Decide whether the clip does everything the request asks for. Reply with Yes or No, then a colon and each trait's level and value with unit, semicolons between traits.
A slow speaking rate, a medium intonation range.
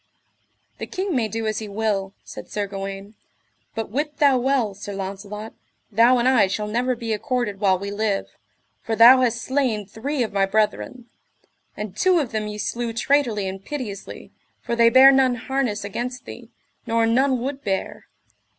No: average, 175 wpm; average, 3.9 semitones